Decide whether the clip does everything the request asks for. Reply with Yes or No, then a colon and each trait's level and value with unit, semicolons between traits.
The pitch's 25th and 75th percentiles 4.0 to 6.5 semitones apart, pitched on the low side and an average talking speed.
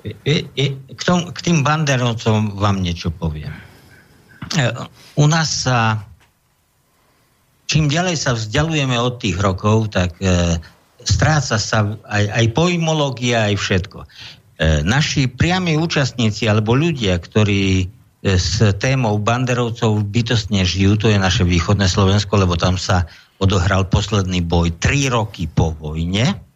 Yes: wide, 5.5 semitones; low, 110 Hz; average, 120 wpm